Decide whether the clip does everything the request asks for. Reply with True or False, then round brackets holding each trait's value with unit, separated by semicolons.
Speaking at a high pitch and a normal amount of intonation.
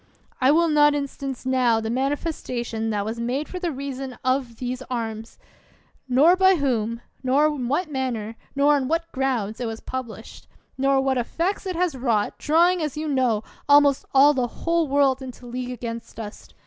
True (265 Hz; 3.7 semitones)